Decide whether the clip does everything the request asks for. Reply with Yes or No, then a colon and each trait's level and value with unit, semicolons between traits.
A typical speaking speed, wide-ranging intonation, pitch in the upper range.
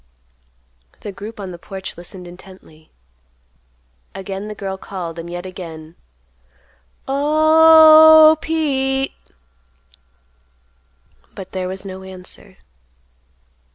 No: slow, 90 wpm; wide, 7.3 semitones; high, 195 Hz